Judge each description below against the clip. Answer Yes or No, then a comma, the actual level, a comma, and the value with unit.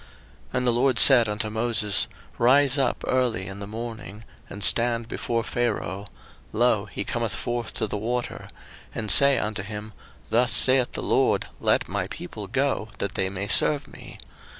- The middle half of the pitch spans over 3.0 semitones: No, average, 2.7 semitones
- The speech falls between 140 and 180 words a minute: Yes, average, 170 wpm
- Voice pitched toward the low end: Yes, low, 115 Hz